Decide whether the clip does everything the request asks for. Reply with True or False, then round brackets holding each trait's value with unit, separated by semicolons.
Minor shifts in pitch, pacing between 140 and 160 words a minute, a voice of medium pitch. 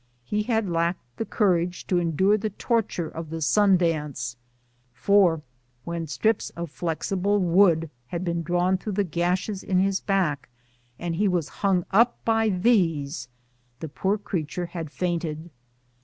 False (3.4 semitones; 150 wpm; 180 Hz)